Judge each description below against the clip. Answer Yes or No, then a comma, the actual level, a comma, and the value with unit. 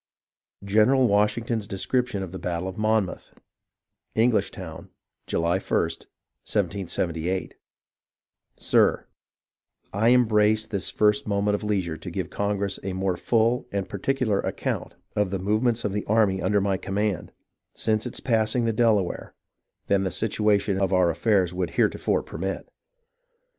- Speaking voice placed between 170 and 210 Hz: No, low, 100 Hz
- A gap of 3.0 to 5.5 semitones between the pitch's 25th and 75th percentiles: No, narrow, 2.5 semitones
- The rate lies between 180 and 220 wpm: No, slow, 135 wpm